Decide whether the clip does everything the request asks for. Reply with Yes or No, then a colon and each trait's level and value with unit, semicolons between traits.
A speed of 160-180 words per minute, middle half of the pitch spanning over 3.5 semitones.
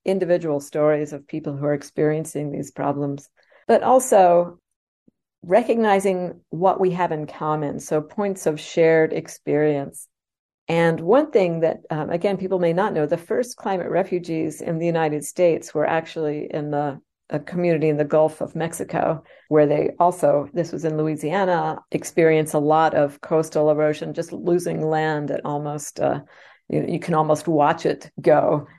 No: average, 165 wpm; narrow, 2.4 semitones